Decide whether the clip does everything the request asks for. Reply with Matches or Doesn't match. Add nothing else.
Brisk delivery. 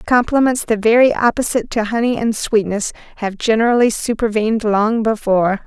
Doesn't match